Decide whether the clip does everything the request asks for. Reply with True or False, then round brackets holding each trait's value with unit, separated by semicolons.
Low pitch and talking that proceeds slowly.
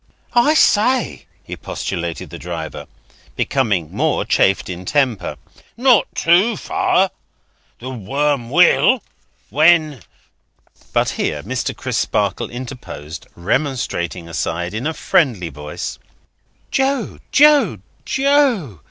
True (130 Hz; 100 wpm)